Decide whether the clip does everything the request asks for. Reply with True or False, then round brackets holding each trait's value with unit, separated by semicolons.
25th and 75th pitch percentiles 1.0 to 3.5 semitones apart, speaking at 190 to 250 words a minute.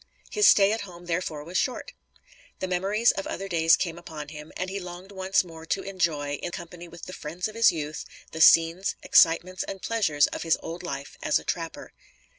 True (2.9 semitones; 205 wpm)